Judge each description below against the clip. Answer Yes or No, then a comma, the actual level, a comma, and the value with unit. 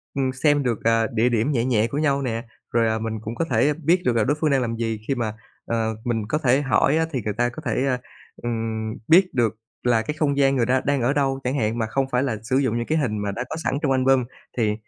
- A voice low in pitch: Yes, low, 125 Hz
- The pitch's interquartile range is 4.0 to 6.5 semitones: No, average, 3.4 semitones